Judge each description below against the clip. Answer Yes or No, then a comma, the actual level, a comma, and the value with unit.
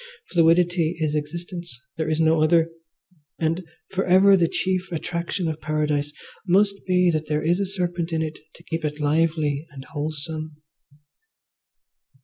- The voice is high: No, medium, 165 Hz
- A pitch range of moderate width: No, narrow, 2.3 semitones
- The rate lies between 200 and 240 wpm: No, average, 145 wpm